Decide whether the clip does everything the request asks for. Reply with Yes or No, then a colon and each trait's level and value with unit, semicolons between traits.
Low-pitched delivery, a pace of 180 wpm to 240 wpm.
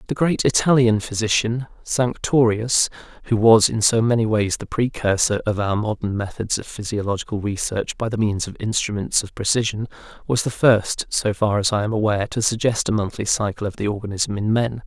Yes: low, 110 Hz; average, 185 wpm